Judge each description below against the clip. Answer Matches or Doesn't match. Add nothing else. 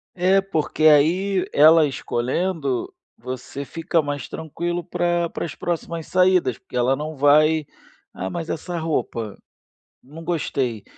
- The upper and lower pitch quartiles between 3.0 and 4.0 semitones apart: Matches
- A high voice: Doesn't match